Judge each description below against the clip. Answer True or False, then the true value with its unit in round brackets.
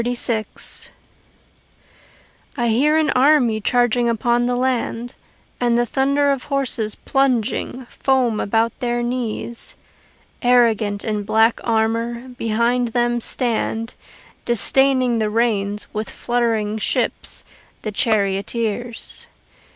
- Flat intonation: True (2.0 semitones)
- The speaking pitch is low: False (235 Hz)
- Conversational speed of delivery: False (105 wpm)